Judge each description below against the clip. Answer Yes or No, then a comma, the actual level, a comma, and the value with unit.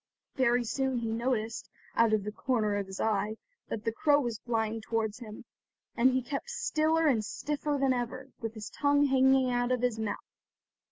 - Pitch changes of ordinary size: Yes, average, 3.3 semitones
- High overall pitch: Yes, high, 240 Hz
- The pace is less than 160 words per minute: No, average, 185 wpm